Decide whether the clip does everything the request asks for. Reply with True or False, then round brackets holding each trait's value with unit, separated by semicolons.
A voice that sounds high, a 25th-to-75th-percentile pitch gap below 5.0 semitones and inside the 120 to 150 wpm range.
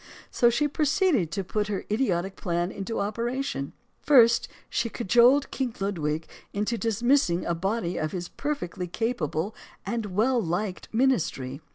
False (215 Hz; 5.4 semitones; 140 wpm)